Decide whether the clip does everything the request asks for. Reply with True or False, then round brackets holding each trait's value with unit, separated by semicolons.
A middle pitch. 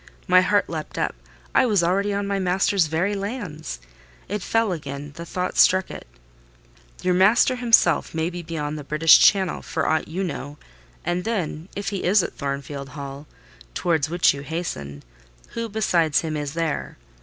True (170 Hz)